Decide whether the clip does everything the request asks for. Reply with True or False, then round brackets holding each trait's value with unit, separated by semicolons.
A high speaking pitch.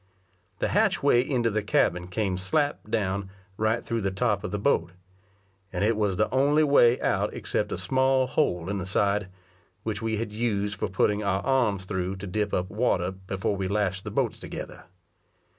False (105 Hz)